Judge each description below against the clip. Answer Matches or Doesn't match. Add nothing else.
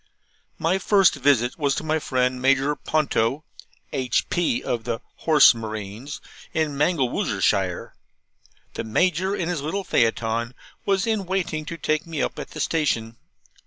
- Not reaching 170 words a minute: Matches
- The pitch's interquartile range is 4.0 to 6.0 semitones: Matches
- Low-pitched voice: Doesn't match